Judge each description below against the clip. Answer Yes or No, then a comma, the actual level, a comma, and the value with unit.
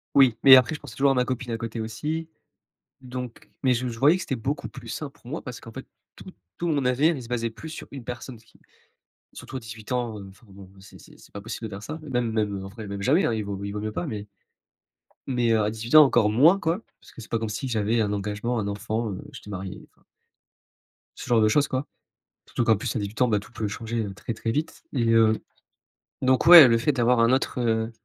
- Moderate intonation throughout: Yes, average, 3.4 semitones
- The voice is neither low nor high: No, low, 115 Hz